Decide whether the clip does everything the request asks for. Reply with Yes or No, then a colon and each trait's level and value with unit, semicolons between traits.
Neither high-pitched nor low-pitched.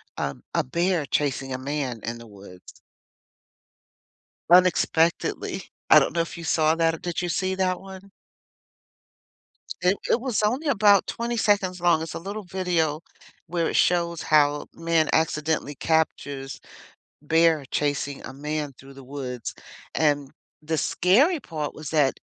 Yes: medium, 160 Hz